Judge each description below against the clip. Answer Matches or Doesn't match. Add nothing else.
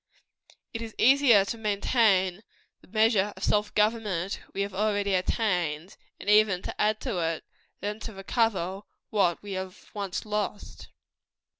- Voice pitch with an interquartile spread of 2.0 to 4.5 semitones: Matches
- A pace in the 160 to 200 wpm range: Doesn't match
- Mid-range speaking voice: Doesn't match